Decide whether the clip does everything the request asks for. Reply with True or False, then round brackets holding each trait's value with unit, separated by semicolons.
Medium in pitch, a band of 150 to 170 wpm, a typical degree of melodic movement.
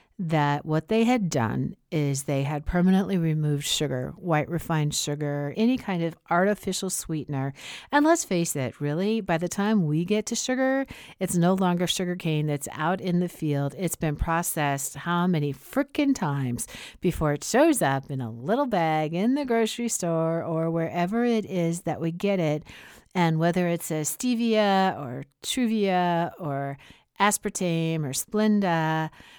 True (170 Hz; 160 wpm; 4.6 semitones)